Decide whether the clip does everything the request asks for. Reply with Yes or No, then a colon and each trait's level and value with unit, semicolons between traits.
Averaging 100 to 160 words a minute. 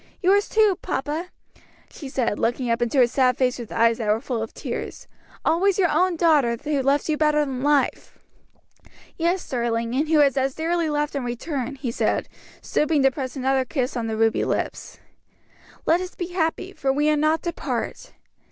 No: average, 190 wpm